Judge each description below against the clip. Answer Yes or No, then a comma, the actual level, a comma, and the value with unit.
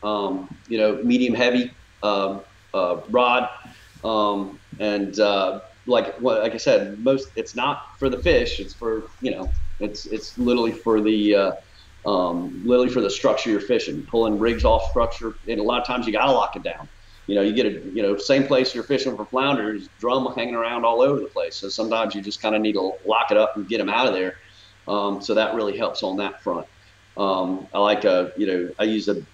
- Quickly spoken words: Yes, fast, 220 wpm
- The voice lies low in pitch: Yes, low, 105 Hz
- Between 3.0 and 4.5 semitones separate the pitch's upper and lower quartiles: No, narrow, 2.6 semitones